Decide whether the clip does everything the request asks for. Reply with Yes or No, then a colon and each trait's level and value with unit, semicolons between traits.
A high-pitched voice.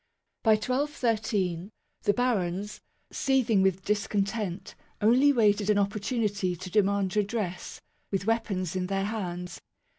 Yes: high, 205 Hz